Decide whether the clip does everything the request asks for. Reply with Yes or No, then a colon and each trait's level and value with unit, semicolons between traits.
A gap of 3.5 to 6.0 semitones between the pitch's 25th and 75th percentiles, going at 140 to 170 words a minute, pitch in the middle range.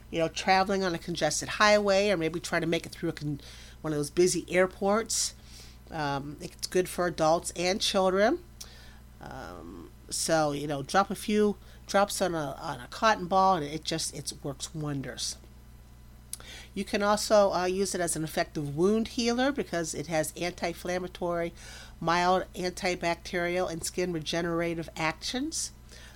Yes: average, 4.4 semitones; average, 160 wpm; medium, 170 Hz